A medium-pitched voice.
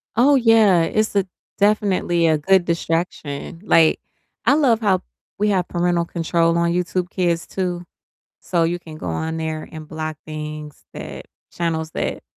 Yes: medium, 170 Hz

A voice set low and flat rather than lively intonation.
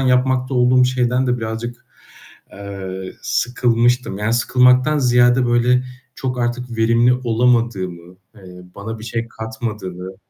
Yes: low, 120 Hz; narrow, 2.2 semitones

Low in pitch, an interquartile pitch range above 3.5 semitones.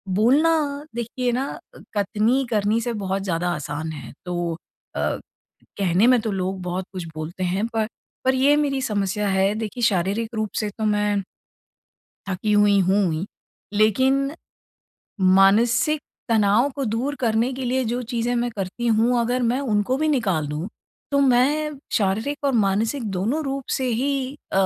No: high, 225 Hz; average, 4.7 semitones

